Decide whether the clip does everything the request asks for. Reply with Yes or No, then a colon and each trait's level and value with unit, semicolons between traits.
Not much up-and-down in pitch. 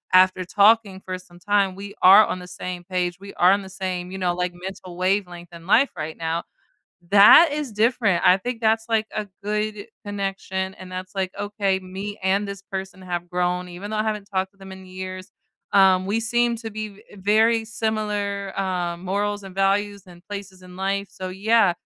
Yes: narrow, 2.0 semitones